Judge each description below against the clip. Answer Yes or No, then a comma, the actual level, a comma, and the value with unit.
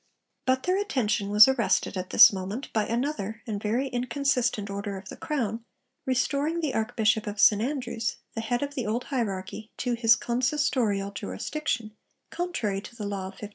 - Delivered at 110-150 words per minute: No, average, 175 wpm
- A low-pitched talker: No, high, 230 Hz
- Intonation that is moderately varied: Yes, average, 4.0 semitones